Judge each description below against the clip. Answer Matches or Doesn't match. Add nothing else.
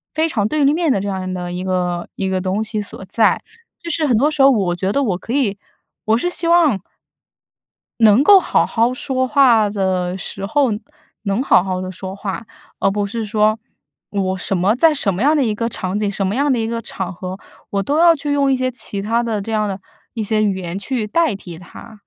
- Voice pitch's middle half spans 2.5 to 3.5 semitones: Doesn't match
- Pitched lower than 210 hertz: Doesn't match